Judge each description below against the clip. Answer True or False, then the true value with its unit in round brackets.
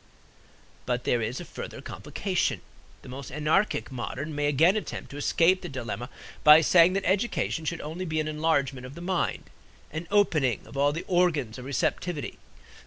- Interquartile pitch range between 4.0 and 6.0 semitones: True (4.4 semitones)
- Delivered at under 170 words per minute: False (175 wpm)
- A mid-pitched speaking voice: True (155 Hz)